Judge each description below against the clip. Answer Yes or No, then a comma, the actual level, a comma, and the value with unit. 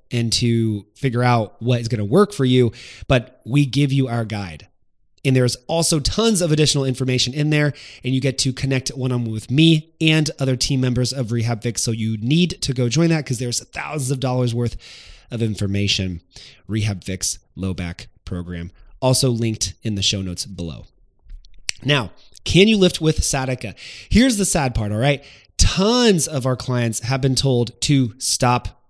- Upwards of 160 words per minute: Yes, average, 185 wpm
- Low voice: Yes, low, 125 Hz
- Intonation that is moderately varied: Yes, average, 4.3 semitones